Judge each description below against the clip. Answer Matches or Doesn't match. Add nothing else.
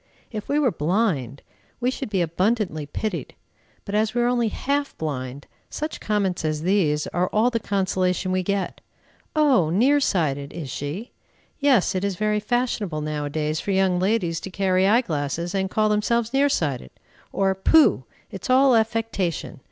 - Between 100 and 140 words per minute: Doesn't match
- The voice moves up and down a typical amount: Doesn't match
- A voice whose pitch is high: Matches